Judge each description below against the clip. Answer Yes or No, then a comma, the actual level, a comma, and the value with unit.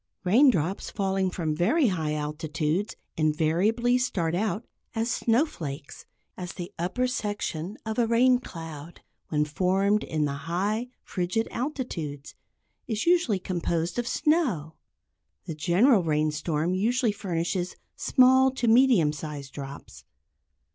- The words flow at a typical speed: No, slow, 120 wpm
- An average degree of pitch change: No, wide, 6.6 semitones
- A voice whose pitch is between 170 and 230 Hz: Yes, medium, 185 Hz